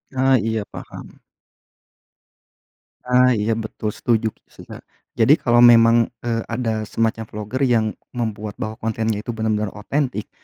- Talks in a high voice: No, low, 115 Hz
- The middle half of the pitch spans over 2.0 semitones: No, narrow, 1.7 semitones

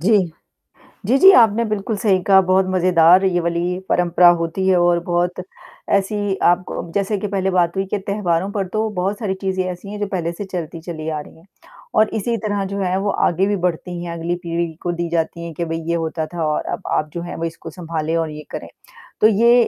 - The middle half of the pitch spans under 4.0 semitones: Yes, average, 2.7 semitones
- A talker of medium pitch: Yes, medium, 180 Hz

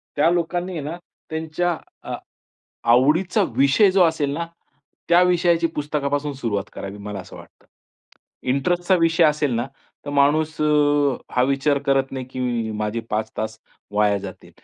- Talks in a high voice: No, medium, 145 Hz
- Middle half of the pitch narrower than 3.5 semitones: No, average, 5.0 semitones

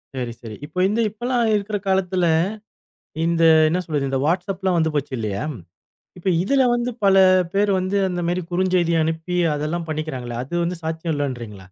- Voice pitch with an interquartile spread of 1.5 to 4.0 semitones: No, average, 4.5 semitones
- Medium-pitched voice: Yes, medium, 170 Hz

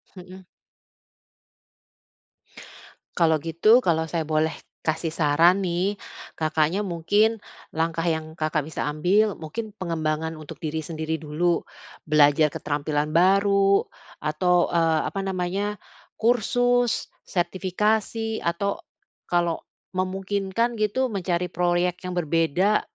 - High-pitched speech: No, medium, 175 Hz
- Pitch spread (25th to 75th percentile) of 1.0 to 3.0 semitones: No, average, 3.8 semitones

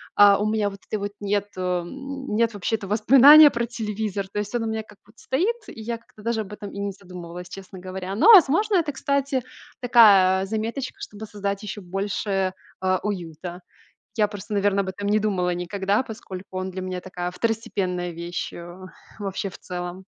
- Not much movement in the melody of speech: No, average, 3.2 semitones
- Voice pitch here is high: Yes, high, 205 Hz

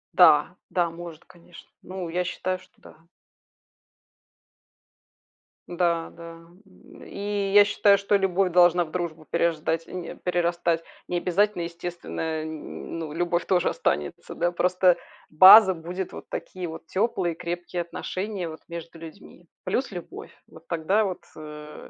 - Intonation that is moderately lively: No, narrow, 1.9 semitones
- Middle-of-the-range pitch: Yes, medium, 175 Hz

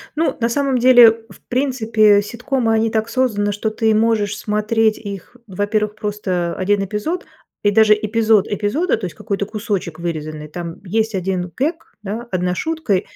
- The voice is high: Yes, high, 215 Hz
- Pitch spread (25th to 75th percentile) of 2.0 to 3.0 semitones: Yes, narrow, 2.5 semitones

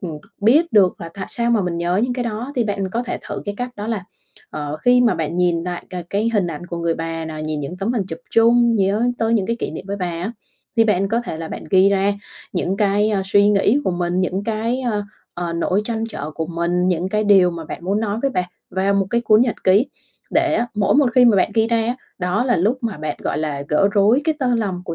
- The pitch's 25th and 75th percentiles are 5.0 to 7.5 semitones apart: No, average, 4.5 semitones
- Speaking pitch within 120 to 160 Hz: No, high, 200 Hz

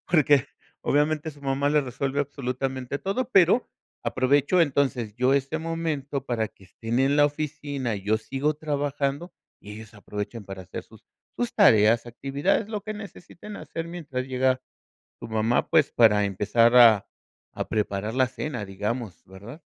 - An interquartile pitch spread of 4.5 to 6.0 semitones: Yes, average, 4.9 semitones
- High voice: No, low, 135 Hz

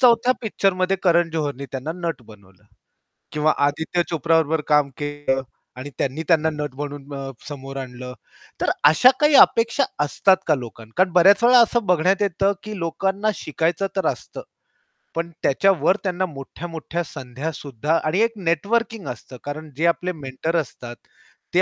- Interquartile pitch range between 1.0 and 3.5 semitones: No, average, 4.9 semitones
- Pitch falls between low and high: Yes, medium, 160 Hz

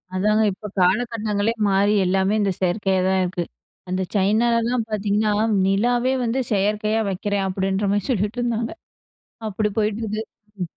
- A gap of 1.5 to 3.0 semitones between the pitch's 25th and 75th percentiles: Yes, narrow, 2.4 semitones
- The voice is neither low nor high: No, high, 210 Hz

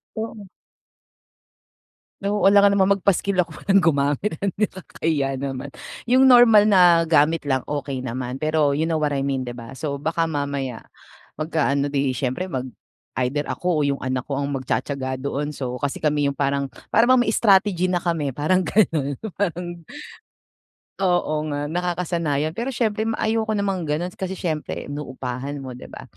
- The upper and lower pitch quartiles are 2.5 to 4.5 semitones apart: No, average, 5.2 semitones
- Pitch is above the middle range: No, medium, 155 Hz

